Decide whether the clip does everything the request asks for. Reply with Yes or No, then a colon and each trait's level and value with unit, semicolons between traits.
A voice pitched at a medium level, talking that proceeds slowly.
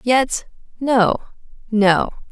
No: high, 225 Hz; slow, 80 wpm